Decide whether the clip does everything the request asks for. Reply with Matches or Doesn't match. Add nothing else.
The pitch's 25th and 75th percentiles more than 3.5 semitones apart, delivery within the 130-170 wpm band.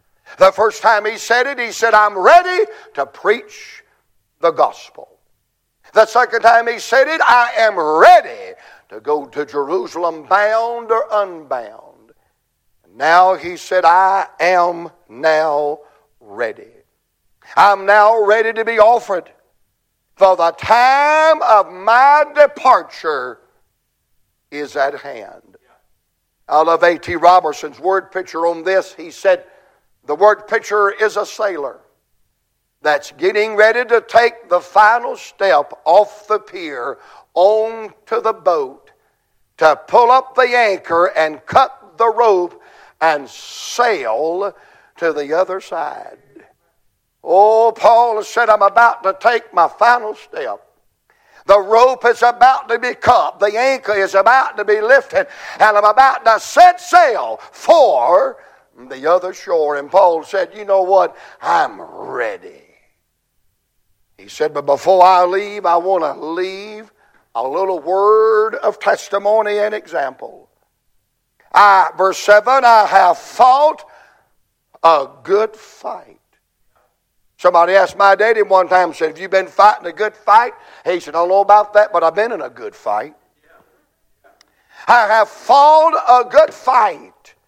Matches